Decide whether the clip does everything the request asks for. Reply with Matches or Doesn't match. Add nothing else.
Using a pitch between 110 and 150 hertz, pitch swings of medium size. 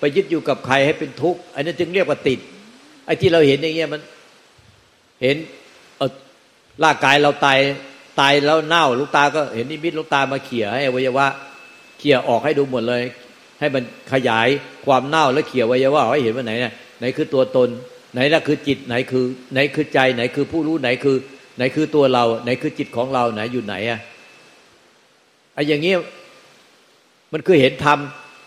Matches